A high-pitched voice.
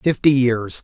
No: low, 125 Hz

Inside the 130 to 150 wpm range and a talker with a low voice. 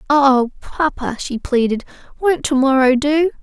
No: average, 140 wpm; very high, 275 Hz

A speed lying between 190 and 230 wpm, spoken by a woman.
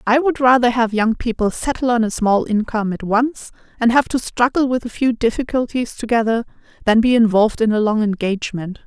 Yes: average, 195 wpm; female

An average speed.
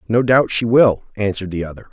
No: fast, 220 wpm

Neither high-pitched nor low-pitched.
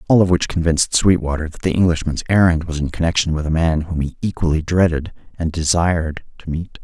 No: very low, 85 Hz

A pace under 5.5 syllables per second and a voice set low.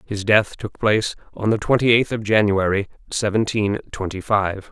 Yes: 4.9 syllables/s; low, 105 Hz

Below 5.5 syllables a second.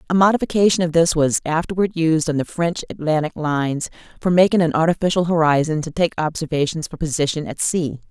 No: 6.0 syllables/s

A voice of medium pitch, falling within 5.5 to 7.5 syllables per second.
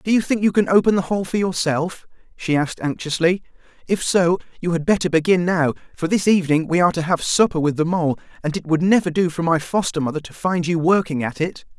Yes: medium, 170 Hz; 6.0 syllables/s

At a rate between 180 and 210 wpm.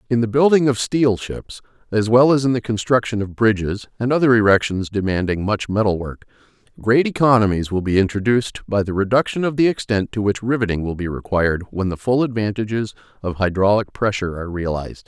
Yes: average, 185 wpm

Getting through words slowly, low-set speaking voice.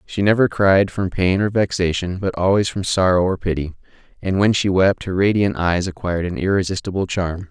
No: average, 190 wpm; very low, 95 Hz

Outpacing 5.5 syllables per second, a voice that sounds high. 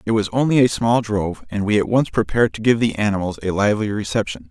No: 6.5 syllables/s; low, 105 Hz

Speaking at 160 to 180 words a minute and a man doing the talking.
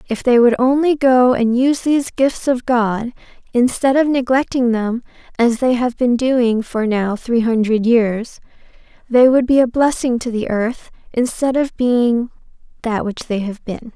No: average, 170 wpm; female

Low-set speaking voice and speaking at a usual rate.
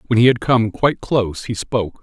No: low, 115 Hz; fast, 240 wpm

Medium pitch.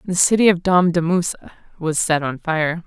Yes: medium, 170 Hz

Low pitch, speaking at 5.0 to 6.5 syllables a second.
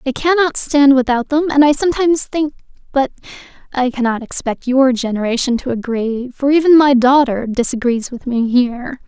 No: very high, 265 Hz; 5.2 syllables/s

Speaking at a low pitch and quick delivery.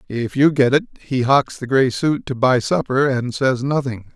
Yes: low, 130 Hz; fast, 215 wpm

